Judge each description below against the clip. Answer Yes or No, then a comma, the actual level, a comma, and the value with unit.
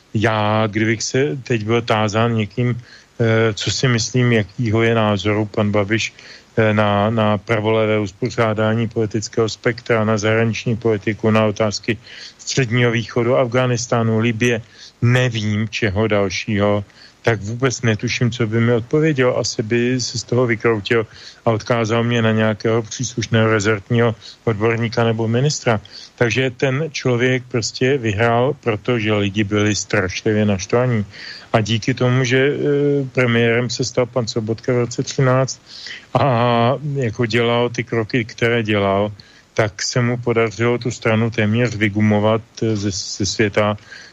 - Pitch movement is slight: Yes, narrow, 2.1 semitones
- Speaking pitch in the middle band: No, low, 115 Hz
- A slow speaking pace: No, average, 130 wpm